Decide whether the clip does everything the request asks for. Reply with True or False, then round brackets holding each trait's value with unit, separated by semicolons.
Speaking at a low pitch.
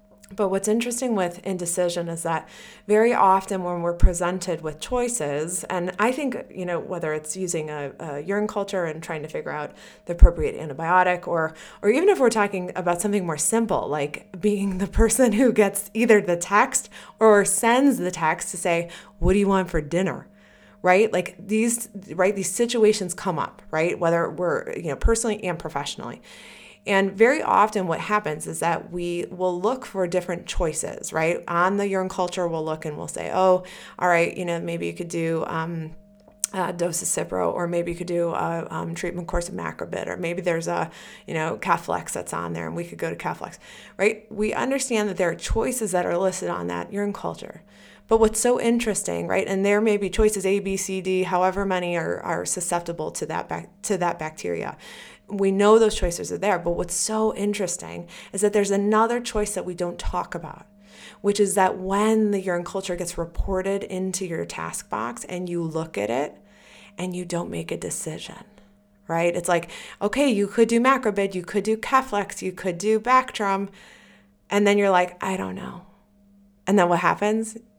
False (185 Hz)